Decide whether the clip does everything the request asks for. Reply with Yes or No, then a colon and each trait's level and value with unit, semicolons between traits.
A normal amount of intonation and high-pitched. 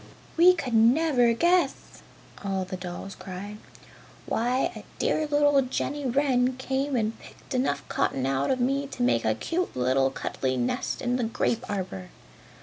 No: wide, 6.6 semitones; high, 245 Hz